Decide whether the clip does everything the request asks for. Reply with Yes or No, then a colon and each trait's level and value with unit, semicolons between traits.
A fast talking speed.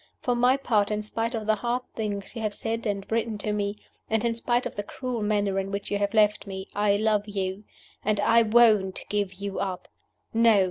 Yes: fast, 220 wpm